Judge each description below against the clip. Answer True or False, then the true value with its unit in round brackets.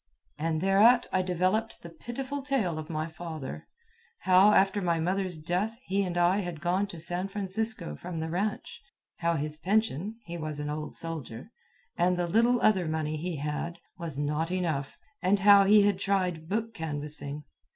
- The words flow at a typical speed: True (170 wpm)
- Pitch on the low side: False (175 Hz)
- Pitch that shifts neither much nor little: True (4.0 semitones)